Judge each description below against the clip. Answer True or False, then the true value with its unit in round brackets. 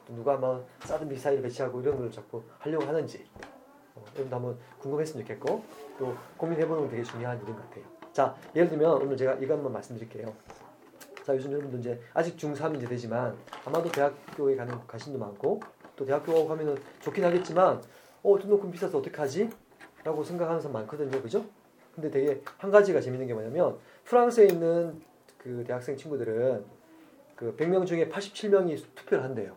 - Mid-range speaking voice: True (150 Hz)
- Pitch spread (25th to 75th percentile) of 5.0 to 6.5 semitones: True (5.6 semitones)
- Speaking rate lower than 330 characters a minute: False (375 characters per minute)